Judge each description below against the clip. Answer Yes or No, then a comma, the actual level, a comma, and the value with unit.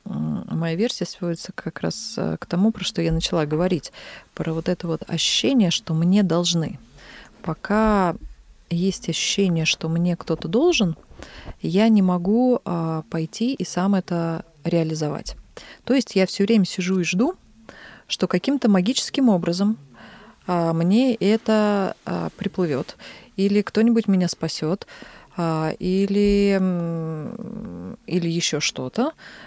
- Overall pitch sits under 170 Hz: No, medium, 185 Hz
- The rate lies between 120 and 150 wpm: Yes, average, 125 wpm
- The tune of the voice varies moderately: Yes, average, 4.4 semitones